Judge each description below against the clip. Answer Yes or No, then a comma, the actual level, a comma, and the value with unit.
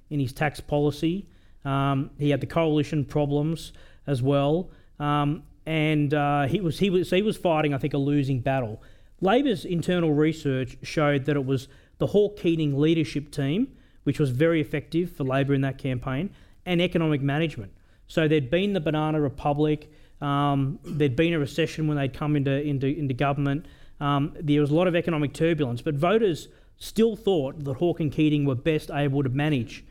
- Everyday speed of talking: Yes, average, 180 wpm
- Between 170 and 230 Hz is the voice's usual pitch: No, medium, 150 Hz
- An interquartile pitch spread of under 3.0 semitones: Yes, narrow, 2.5 semitones